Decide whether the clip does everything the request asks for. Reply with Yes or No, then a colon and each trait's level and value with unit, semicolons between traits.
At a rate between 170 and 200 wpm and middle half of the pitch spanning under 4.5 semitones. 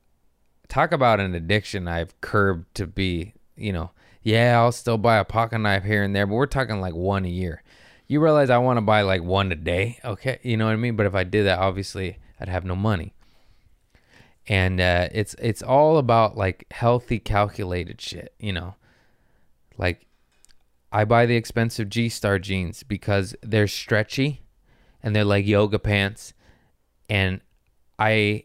Yes: average, 175 wpm; average, 3.5 semitones